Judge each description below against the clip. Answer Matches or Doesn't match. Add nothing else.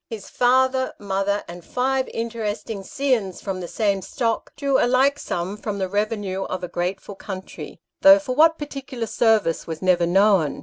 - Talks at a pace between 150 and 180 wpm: Matches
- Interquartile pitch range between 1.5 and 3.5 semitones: Doesn't match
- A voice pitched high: Matches